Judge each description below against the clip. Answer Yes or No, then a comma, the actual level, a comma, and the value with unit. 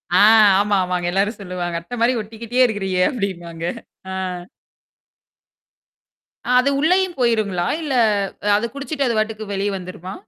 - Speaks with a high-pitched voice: Yes, high, 210 Hz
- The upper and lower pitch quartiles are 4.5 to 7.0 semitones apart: Yes, average, 4.9 semitones